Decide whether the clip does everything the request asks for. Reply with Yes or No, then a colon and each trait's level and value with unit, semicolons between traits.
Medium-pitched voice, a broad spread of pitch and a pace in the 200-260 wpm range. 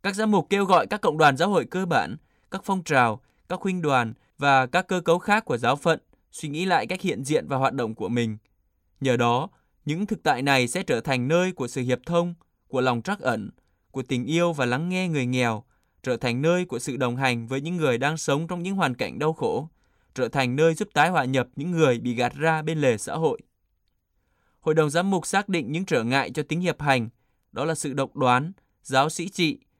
Yes: medium, 145 Hz; wide, 5.7 semitones; average, 240 wpm